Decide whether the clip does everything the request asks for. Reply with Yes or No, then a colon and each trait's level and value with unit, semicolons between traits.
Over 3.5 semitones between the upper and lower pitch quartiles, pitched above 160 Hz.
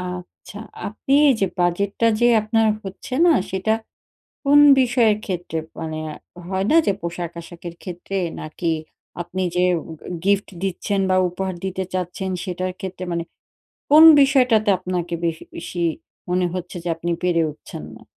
No: average, 3.0 semitones; medium, 185 Hz